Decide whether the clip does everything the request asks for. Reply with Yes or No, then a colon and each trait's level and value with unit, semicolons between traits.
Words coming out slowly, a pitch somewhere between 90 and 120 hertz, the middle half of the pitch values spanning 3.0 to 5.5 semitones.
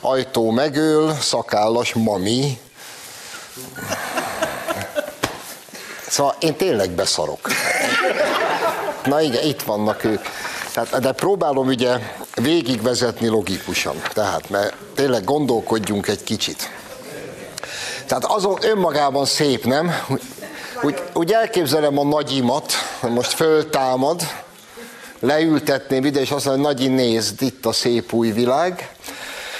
No: slow, 95 wpm; low, 130 Hz; average, 4.2 semitones